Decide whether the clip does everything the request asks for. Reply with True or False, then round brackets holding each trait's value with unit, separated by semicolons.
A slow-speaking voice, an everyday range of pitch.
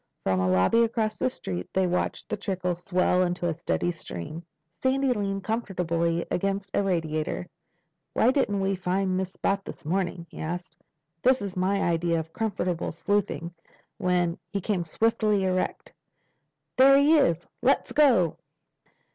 False (150 wpm; 3.3 semitones)